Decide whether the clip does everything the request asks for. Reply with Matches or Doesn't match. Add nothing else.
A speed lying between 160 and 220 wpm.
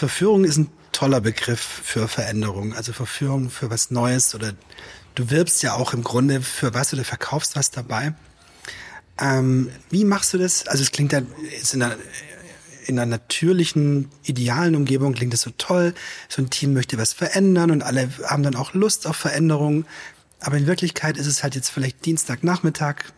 Matches